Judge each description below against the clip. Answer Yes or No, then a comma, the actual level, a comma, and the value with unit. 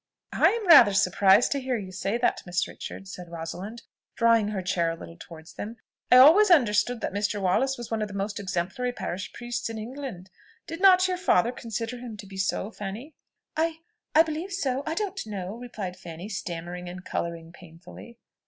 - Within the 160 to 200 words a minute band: Yes, average, 190 wpm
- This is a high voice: Yes, high, 210 Hz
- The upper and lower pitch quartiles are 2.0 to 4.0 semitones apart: No, wide, 5.5 semitones